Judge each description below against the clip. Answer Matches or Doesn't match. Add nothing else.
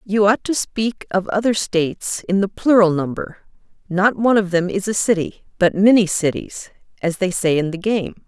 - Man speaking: Doesn't match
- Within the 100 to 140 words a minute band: Doesn't match